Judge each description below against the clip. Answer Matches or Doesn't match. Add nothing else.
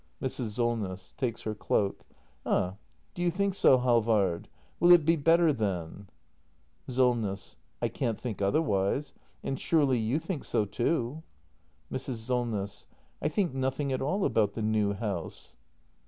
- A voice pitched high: Doesn't match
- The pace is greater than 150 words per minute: Doesn't match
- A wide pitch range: Matches